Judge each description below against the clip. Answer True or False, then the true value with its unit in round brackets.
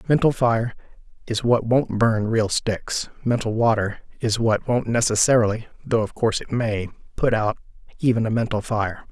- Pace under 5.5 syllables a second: True (4.4 syllables/s)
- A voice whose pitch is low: True (115 Hz)